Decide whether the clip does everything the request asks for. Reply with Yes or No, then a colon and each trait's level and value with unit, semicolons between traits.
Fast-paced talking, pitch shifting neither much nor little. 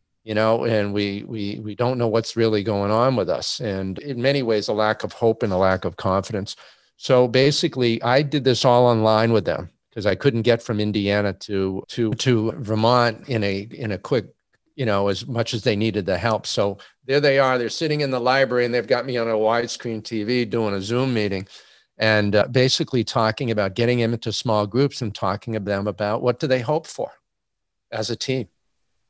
Yes: fast, 215 wpm; average, 3.1 semitones